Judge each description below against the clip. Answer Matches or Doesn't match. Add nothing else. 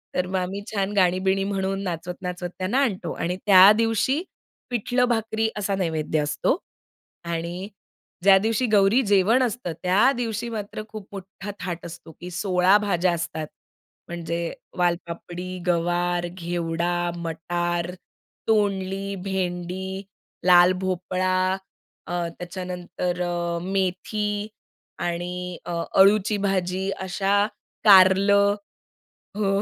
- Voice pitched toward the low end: Doesn't match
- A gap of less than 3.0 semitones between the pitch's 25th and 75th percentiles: Matches